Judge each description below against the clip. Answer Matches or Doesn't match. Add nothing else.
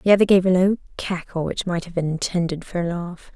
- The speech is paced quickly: Matches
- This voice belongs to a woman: Matches